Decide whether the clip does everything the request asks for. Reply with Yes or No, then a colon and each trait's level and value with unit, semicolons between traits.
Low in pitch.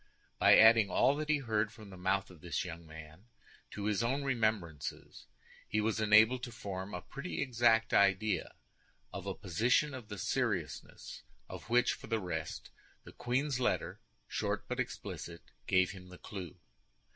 Yes: low, 105 Hz